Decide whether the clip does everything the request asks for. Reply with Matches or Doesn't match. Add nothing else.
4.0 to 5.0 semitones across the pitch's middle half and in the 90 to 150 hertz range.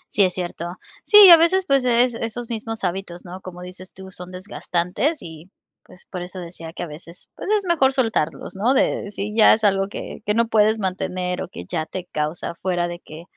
Doesn't match